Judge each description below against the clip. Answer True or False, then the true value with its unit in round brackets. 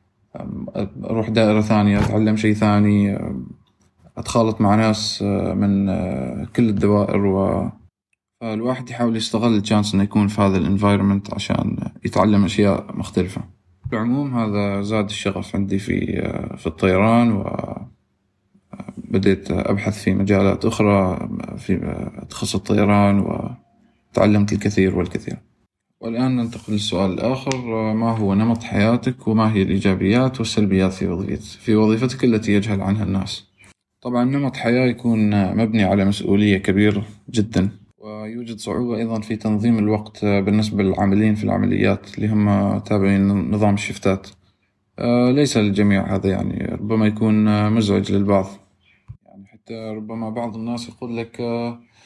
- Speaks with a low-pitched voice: True (105 Hz)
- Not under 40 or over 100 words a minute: False (120 wpm)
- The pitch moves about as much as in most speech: False (2.3 semitones)